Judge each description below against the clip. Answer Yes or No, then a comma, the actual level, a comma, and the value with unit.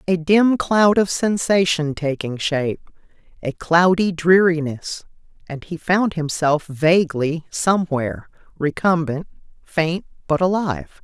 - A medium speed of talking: No, slow, 110 wpm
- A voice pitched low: No, medium, 170 Hz